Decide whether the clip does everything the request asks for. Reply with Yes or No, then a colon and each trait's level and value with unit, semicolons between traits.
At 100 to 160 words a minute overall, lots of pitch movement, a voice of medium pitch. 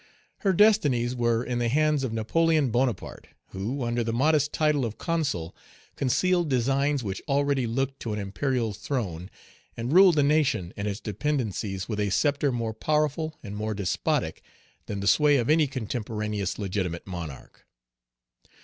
No: average, 155 wpm; wide, 5.7 semitones; low, 125 Hz